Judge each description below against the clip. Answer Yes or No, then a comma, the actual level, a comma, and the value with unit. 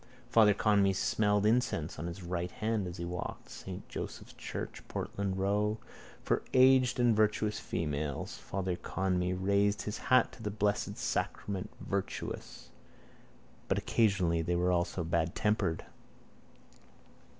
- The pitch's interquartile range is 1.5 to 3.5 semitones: Yes, average, 3.1 semitones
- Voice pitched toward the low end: Yes, low, 100 Hz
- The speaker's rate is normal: No, slow, 130 wpm